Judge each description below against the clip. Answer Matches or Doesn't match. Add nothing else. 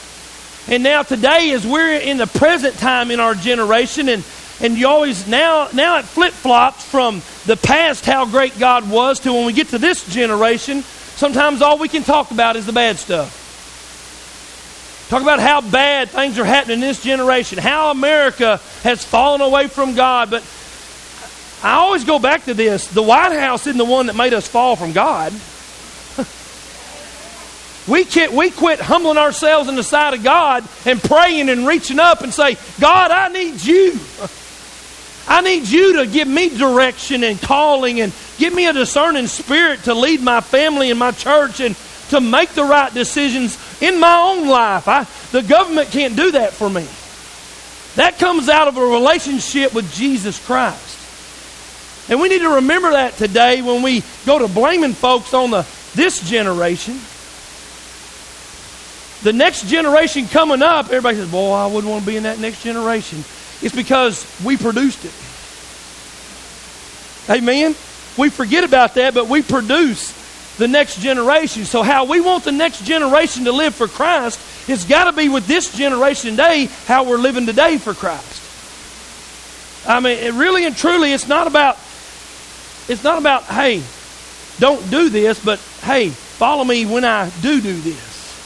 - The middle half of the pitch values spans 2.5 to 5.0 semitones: Matches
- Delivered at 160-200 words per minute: Matches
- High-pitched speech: Matches